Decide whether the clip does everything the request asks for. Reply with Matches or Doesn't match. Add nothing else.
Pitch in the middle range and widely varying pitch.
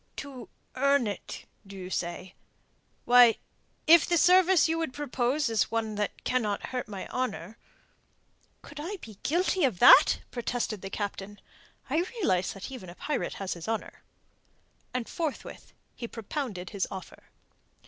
Doesn't match